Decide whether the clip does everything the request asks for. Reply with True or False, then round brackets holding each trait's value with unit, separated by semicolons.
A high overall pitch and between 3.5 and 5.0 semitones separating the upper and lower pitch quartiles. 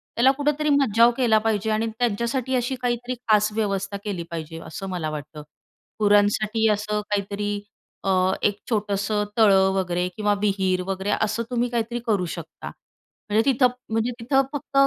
False (210 Hz; 3.1 semitones)